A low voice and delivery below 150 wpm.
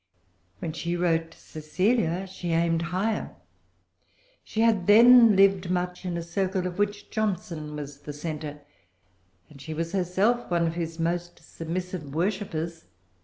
No: medium, 175 Hz; average, 140 wpm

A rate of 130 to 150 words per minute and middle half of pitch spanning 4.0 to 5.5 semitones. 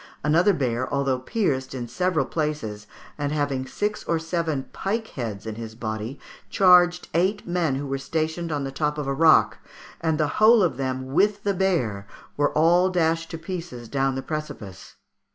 No: average, 175 wpm; average, 5.0 semitones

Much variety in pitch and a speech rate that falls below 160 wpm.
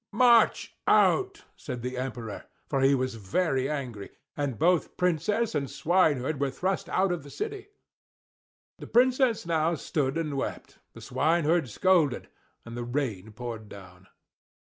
Yes: wide, 6.3 semitones; average, 145 wpm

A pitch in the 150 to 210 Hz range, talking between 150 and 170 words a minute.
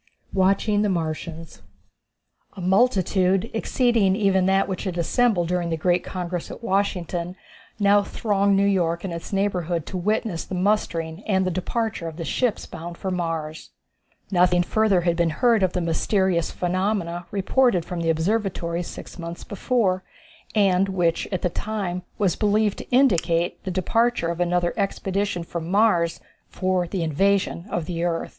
Yes: medium, 185 Hz; average, 160 wpm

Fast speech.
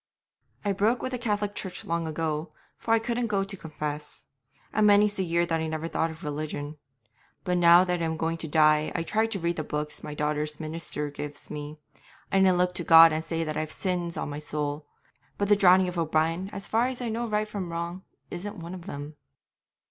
Yes: fast, 220 wpm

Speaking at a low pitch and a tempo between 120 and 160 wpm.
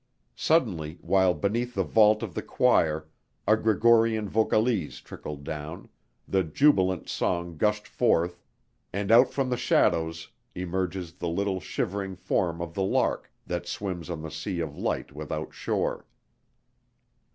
Yes: very low, 95 Hz; average, 140 wpm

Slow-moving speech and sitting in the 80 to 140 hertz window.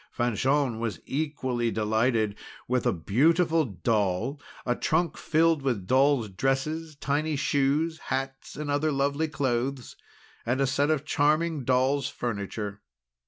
Yes: slow, 125 wpm; low, 135 Hz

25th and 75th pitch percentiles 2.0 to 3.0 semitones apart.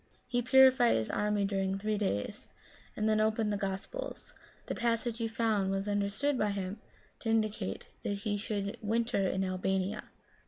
Yes: narrow, 2.5 semitones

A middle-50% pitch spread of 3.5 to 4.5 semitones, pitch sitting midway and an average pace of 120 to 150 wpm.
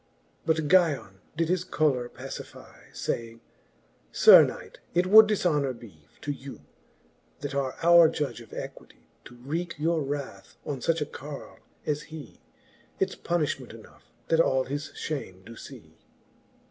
Yes: average, 4.2 semitones; medium, 145 Hz; average, 145 wpm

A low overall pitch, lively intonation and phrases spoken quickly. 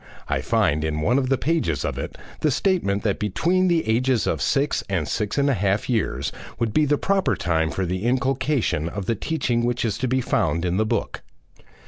Yes: low, 120 Hz; wide, 6.5 semitones; fast, 210 wpm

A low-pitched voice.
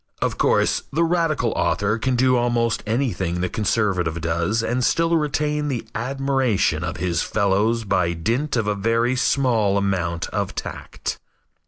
Yes: low, 115 Hz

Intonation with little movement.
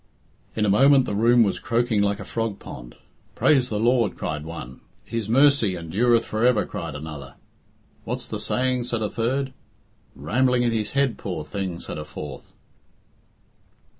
No: average, 5.0 semitones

